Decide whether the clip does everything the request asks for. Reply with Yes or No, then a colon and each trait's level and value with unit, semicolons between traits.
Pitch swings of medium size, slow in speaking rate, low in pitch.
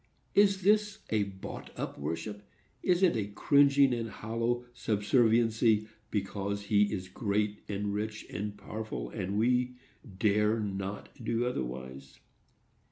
Yes: average, 3.1 semitones; slow, 120 wpm; low, 105 Hz